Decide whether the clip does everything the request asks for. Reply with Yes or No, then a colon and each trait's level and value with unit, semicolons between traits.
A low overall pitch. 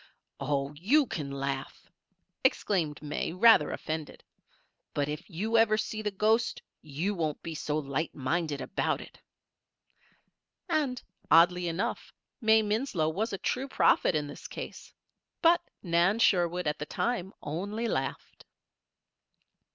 No: medium, 175 Hz